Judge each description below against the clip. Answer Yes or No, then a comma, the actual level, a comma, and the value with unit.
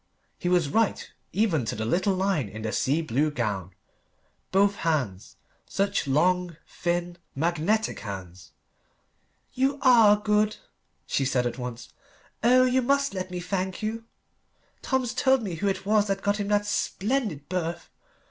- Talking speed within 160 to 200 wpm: No, average, 150 wpm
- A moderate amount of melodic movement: No, wide, 6.8 semitones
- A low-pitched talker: No, medium, 185 Hz